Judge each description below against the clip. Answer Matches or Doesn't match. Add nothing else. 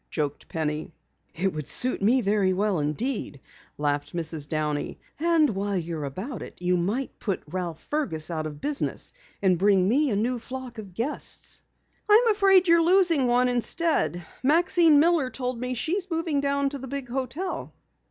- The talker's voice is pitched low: Doesn't match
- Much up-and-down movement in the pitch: Matches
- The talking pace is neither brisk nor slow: Matches